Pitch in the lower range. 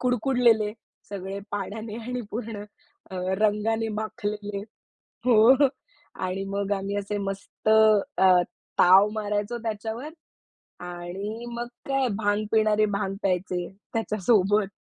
No: high, 210 Hz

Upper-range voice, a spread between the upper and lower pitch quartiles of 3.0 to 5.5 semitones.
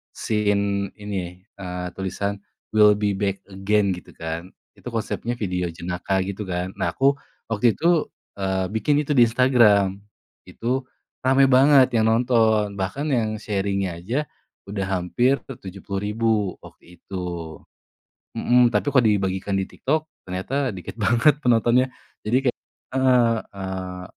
No: low, 105 Hz; average, 4.2 semitones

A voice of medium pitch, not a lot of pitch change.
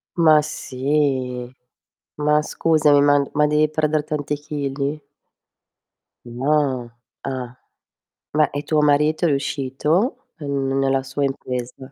Yes: medium, 145 Hz; narrow, 2.1 semitones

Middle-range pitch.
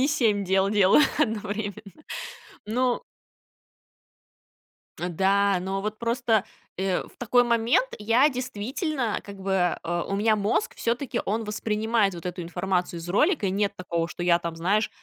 No: high, 205 Hz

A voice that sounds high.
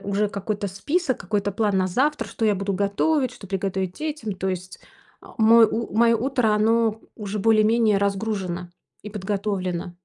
Yes: high, 210 Hz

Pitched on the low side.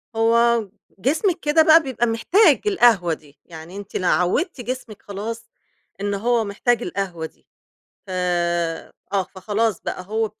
No: high, 225 Hz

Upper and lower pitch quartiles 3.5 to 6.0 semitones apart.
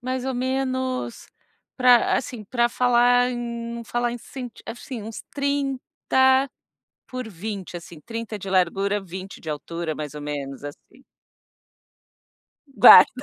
Yes: average, 5.1 semitones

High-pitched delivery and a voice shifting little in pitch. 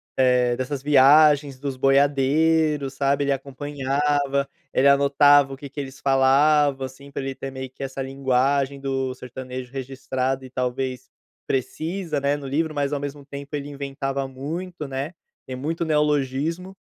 No: medium, 140 Hz; narrow, 1.6 semitones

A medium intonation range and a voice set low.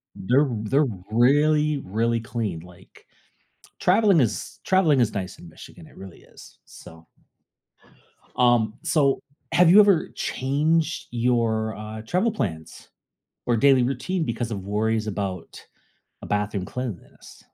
No: wide, 6.0 semitones; low, 120 Hz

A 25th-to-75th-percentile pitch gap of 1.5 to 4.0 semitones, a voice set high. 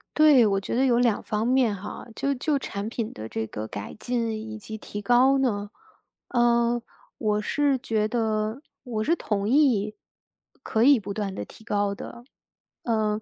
Yes: average, 2.9 semitones; high, 220 Hz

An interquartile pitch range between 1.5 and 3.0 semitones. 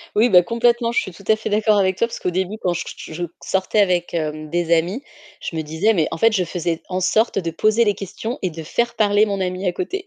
No: average, 4.0 semitones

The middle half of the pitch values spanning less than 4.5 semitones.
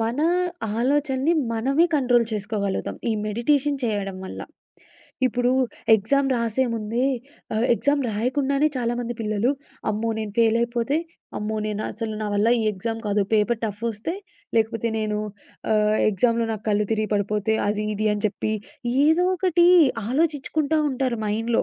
Yes: average, 3.6 semitones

